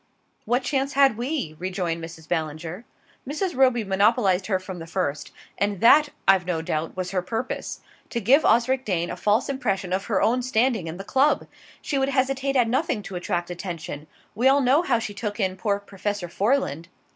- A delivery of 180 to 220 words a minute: Yes, average, 190 wpm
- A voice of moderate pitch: No, high, 205 Hz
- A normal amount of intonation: No, wide, 6.3 semitones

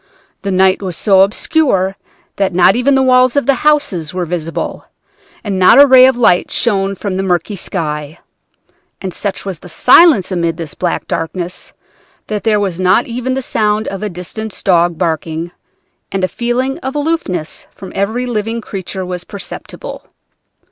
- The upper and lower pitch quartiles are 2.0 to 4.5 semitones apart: No, average, 5.1 semitones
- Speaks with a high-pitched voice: Yes, high, 195 Hz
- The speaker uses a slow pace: No, average, 170 wpm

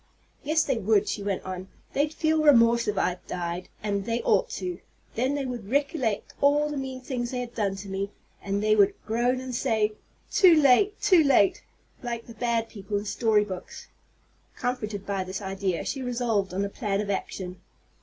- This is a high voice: Yes, high, 225 Hz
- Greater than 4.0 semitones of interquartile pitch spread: Yes, average, 4.6 semitones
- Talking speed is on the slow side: No, average, 185 wpm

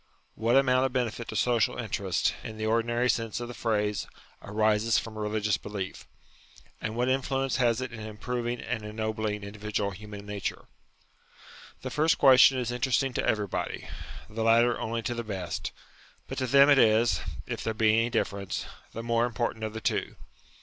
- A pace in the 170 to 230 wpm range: Yes, average, 175 wpm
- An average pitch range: No, narrow, 2.3 semitones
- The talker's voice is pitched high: No, low, 115 Hz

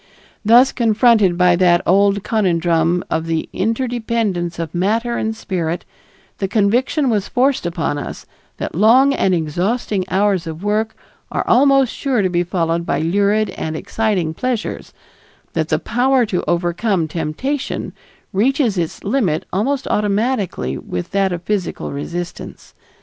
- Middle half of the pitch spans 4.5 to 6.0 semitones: Yes, average, 5.0 semitones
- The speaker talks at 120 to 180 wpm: Yes, average, 140 wpm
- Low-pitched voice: No, high, 200 Hz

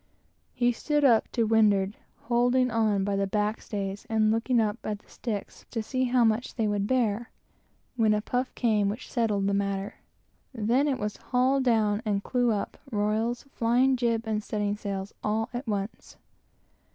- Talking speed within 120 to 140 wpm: No, average, 170 wpm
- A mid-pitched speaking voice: No, high, 220 Hz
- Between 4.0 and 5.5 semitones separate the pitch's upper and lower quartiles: No, average, 2.8 semitones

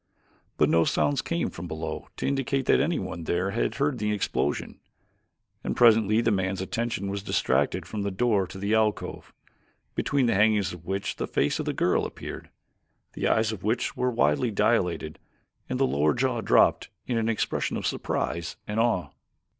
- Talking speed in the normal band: Yes, average, 170 wpm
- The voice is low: Yes, low, 105 Hz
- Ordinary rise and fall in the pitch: Yes, average, 4.2 semitones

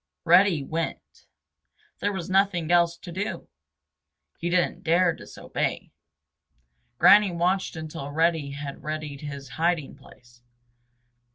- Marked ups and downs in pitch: No, average, 3.0 semitones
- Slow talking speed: Yes, slow, 110 wpm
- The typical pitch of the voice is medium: Yes, medium, 165 Hz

